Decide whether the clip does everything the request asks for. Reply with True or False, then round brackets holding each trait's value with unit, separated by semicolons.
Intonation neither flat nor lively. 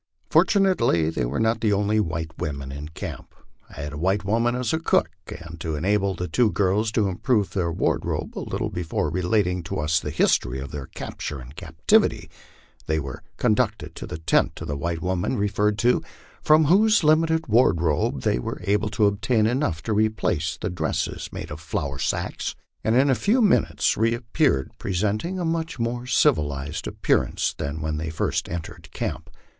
False (6.7 semitones)